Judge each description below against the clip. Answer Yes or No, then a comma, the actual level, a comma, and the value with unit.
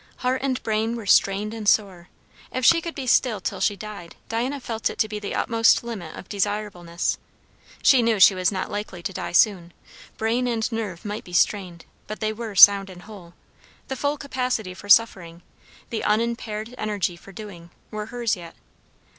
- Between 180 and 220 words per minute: Yes, average, 185 wpm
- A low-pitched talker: No, high, 210 Hz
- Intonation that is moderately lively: Yes, average, 3.5 semitones